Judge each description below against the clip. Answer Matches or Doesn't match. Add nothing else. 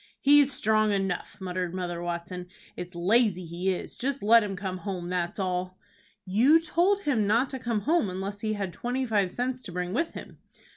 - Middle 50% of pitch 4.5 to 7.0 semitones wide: Matches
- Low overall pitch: Doesn't match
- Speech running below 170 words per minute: Doesn't match